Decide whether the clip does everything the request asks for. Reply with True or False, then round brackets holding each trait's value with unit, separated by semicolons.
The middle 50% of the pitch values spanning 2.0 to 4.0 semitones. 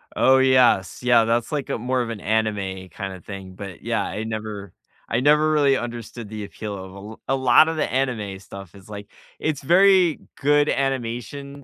False (5.0 semitones)